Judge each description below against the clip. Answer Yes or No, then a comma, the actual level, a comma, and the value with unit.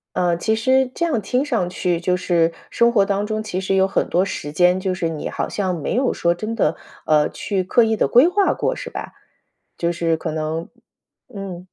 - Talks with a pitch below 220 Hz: Yes, high, 190 Hz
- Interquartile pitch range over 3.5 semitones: Yes, average, 4.6 semitones